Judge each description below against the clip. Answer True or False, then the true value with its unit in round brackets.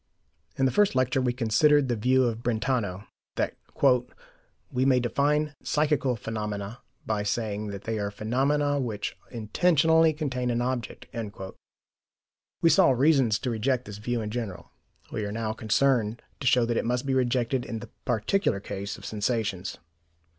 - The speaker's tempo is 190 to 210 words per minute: False (155 wpm)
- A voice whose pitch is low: True (120 Hz)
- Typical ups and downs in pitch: True (3.7 semitones)